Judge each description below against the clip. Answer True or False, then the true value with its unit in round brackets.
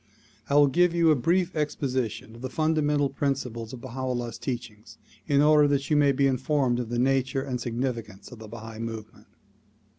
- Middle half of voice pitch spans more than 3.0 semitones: True (3.7 semitones)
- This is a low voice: True (130 Hz)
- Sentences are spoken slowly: False (190 wpm)